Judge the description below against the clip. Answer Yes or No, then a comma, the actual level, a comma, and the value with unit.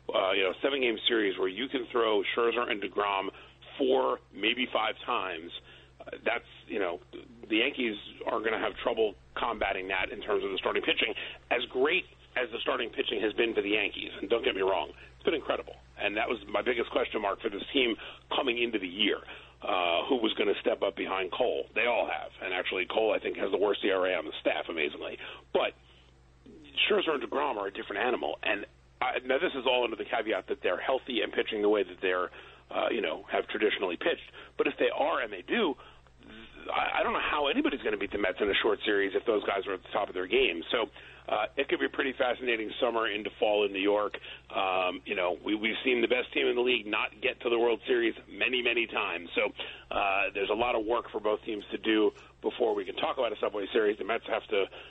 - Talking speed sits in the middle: No, fast, 240 wpm